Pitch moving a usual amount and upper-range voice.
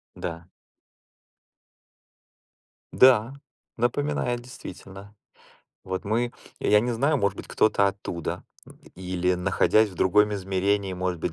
No: average, 4.0 semitones; low, 100 Hz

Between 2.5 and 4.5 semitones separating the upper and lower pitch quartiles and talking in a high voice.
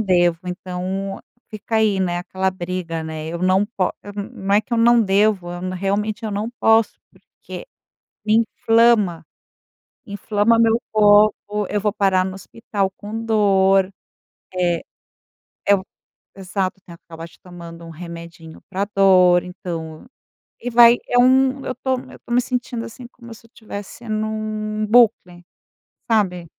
Yes: average, 3.5 semitones; high, 200 Hz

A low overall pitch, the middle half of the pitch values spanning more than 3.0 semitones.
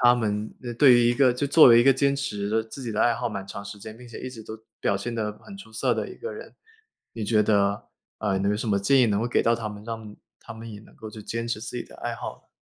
No: low, 115 Hz; average, 2.7 semitones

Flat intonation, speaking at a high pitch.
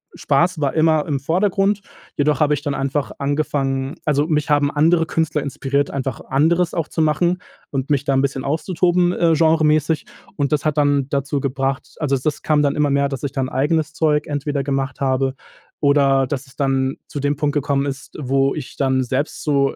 No: narrow, 2.1 semitones; medium, 145 Hz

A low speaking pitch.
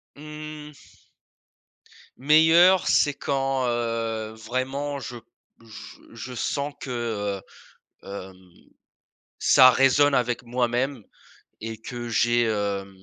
Yes: low, 120 Hz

